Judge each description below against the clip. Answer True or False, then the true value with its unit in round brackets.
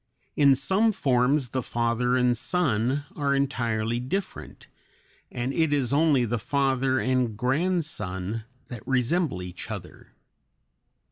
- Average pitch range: True (3.3 semitones)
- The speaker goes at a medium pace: False (120 wpm)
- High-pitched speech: False (130 Hz)